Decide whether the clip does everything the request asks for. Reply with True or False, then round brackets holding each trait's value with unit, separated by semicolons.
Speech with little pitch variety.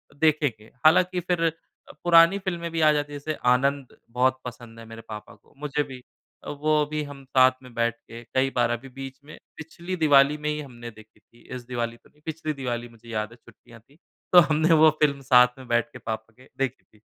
False (4.4 semitones)